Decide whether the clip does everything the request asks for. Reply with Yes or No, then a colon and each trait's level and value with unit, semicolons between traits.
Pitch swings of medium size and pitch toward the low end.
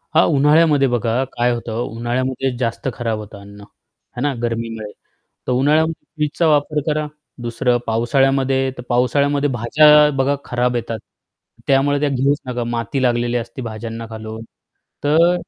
Yes: average, 3.5 semitones; low, 125 Hz